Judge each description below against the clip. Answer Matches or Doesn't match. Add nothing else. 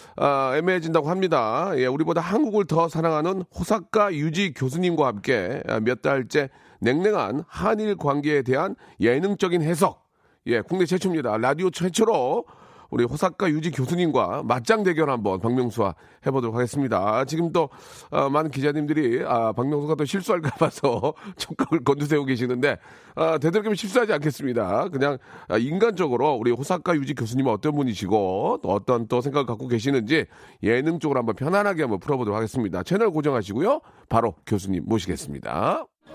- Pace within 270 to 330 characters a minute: Doesn't match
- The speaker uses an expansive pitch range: Matches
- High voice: Doesn't match